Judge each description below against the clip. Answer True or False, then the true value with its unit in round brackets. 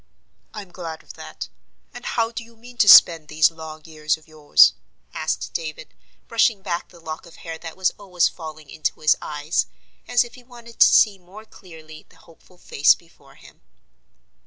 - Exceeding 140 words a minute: True (180 wpm)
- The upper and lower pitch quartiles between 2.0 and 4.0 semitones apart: False (5.0 semitones)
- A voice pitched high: False (170 Hz)